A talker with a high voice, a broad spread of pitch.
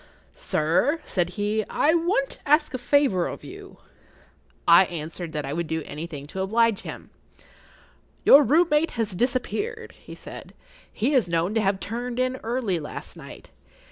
Yes: high, 225 Hz; wide, 8.2 semitones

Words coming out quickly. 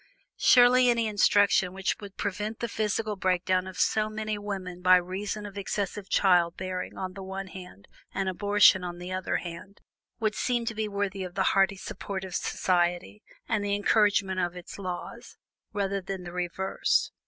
No: average, 175 wpm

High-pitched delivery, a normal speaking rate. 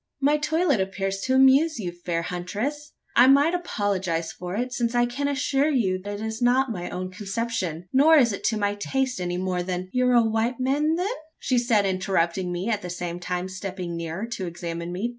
No: high, 205 Hz; fast, 210 wpm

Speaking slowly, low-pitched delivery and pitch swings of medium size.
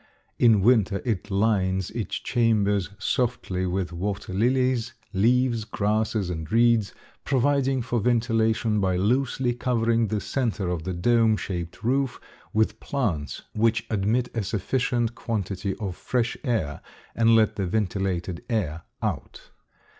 Yes: slow, 130 wpm; low, 110 Hz; average, 3.7 semitones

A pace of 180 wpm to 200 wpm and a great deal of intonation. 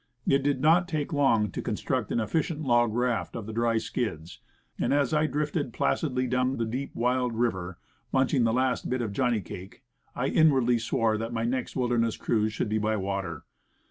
No: average, 190 wpm; average, 3.3 semitones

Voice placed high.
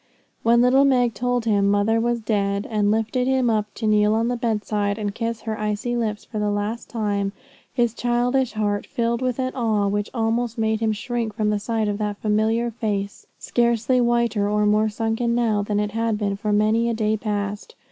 Yes: high, 220 Hz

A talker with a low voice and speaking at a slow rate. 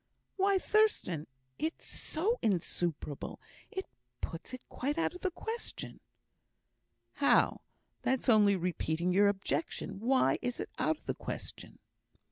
No: high, 245 Hz; slow, 125 wpm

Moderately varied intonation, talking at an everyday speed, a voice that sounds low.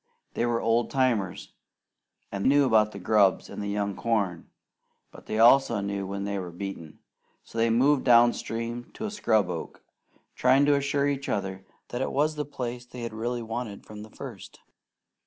Yes: average, 4.1 semitones; average, 185 wpm; low, 115 Hz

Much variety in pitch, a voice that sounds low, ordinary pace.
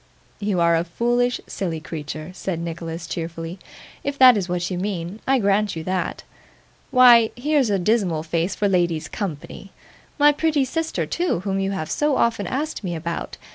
No: wide, 6.2 semitones; high, 195 Hz; average, 175 wpm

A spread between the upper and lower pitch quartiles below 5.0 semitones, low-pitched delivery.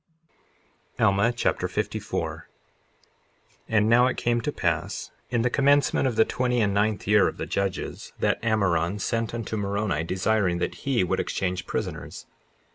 Yes: average, 3.6 semitones; low, 105 Hz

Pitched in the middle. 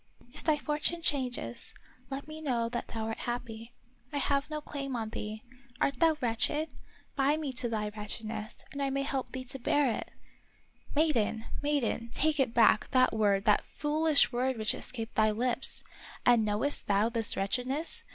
No: very high, 250 Hz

